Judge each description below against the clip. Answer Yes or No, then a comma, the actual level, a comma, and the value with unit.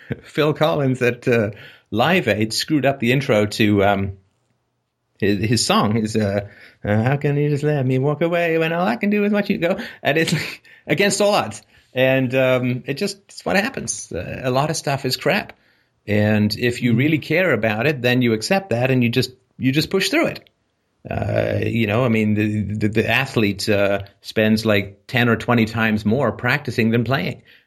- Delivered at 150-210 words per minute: Yes, average, 200 wpm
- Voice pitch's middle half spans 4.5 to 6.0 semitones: Yes, average, 5.1 semitones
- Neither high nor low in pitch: No, low, 125 Hz